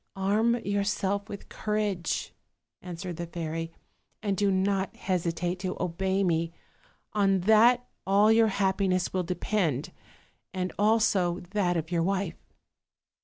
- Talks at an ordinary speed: No, slow, 125 wpm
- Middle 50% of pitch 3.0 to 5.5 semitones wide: No, narrow, 2.5 semitones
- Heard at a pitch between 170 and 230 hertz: Yes, high, 190 Hz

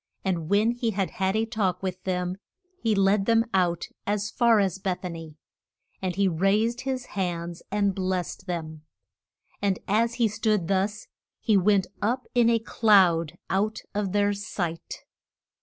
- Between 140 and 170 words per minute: Yes, average, 160 wpm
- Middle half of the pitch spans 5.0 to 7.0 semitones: No, average, 3.0 semitones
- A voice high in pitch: Yes, high, 195 Hz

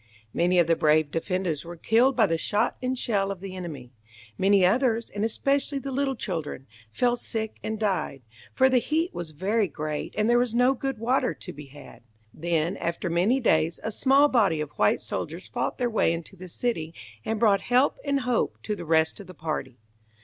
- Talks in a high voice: Yes, high, 200 Hz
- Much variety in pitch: Yes, wide, 6.8 semitones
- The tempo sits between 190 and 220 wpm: Yes, average, 200 wpm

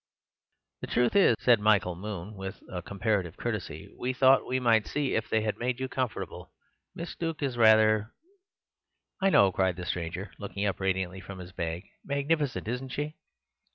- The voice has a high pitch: No, low, 110 Hz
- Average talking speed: Yes, average, 165 wpm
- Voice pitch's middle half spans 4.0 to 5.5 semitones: Yes, average, 5.2 semitones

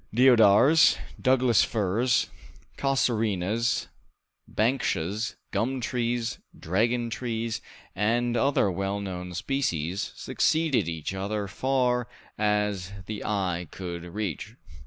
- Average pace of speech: No, slow, 95 wpm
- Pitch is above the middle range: No, low, 110 Hz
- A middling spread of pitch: Yes, average, 4.0 semitones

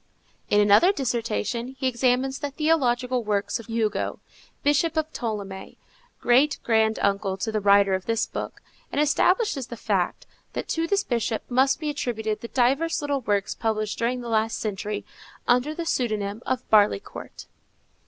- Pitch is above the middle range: Yes, high, 240 Hz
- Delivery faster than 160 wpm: No, average, 155 wpm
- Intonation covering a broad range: No, average, 4.3 semitones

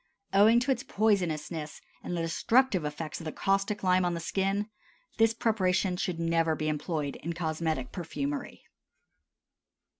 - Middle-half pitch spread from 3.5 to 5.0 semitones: Yes, average, 4.0 semitones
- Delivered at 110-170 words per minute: Yes, average, 145 wpm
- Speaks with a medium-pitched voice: Yes, medium, 175 Hz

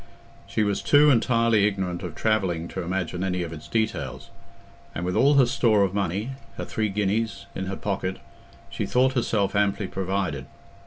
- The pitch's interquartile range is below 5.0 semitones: Yes, average, 3.6 semitones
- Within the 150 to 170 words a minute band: Yes, average, 160 wpm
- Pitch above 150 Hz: No, low, 100 Hz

